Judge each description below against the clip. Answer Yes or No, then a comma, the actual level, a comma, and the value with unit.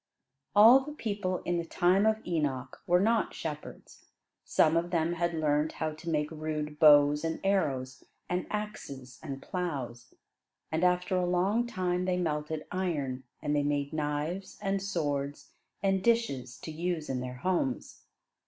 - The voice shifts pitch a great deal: No, average, 3.9 semitones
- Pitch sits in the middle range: Yes, medium, 165 Hz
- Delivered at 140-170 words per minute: Yes, average, 155 wpm